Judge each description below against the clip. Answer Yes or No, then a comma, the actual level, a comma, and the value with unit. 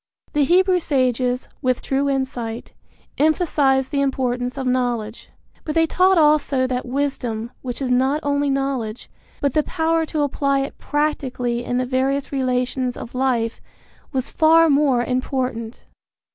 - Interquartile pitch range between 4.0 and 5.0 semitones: No, narrow, 2.5 semitones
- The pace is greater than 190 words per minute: No, average, 145 wpm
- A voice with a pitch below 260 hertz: No, very high, 265 Hz